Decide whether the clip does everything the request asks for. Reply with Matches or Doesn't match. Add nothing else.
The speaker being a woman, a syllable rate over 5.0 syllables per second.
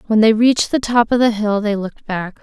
Matches